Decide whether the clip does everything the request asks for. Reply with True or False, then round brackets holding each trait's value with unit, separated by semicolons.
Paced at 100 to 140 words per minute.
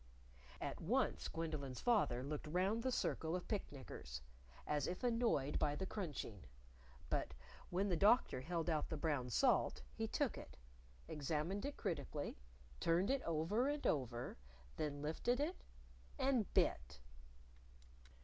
True (135 wpm)